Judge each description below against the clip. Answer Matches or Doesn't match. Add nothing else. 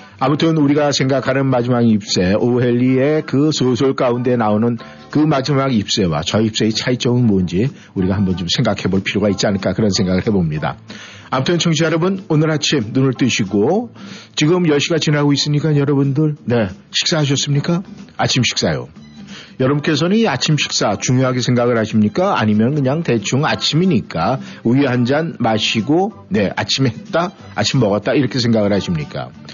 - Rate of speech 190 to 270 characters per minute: Doesn't match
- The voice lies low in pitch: Matches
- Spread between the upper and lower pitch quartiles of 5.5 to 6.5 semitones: Doesn't match